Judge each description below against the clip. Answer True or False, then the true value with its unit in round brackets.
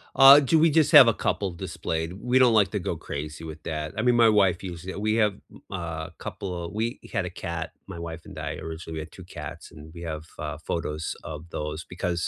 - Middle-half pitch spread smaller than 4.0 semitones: False (5.1 semitones)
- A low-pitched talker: True (85 Hz)